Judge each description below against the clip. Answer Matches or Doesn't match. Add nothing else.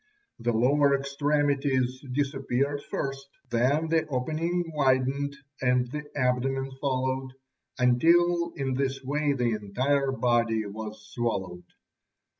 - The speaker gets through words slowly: Matches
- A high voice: Doesn't match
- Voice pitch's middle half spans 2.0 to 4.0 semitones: Matches